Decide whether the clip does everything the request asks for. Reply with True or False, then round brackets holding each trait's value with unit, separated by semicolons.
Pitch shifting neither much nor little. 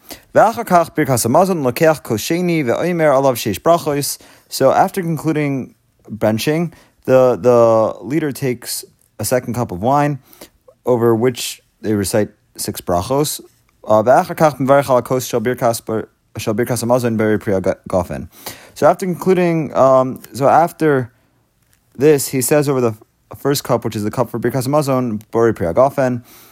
True (4.4 semitones)